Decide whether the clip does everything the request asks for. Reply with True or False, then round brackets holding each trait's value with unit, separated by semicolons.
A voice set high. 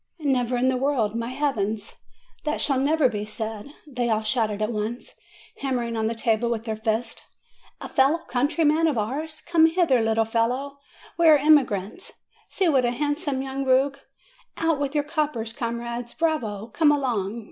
True (255 Hz)